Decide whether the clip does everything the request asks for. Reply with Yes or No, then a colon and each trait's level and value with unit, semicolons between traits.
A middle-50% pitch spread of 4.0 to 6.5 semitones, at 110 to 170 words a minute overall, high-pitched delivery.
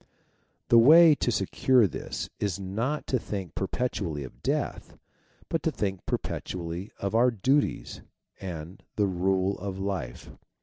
No: average, 4.3 semitones; average, 140 wpm; low, 100 Hz